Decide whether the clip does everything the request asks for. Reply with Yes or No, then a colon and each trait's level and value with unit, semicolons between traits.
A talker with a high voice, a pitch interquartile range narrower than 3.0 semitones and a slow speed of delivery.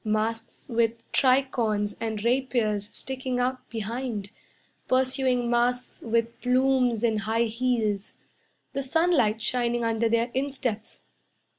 Yes: high, 235 Hz; narrow, 2.5 semitones; slow, 110 wpm